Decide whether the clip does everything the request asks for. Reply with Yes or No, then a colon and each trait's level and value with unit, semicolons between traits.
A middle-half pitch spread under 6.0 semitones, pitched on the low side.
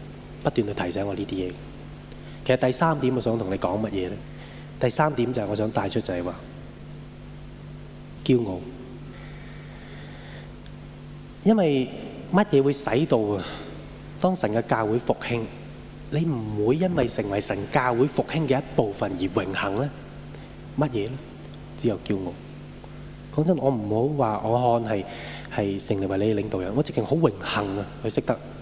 Yes: wide, 5.5 semitones; low, 120 Hz